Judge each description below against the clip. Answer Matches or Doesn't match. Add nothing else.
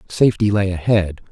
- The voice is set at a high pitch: Doesn't match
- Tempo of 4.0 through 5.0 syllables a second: Doesn't match